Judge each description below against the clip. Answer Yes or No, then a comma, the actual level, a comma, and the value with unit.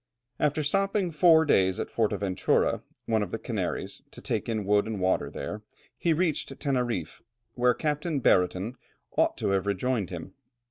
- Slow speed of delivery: No, average, 155 wpm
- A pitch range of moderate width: No, wide, 7.5 semitones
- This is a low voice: Yes, low, 115 Hz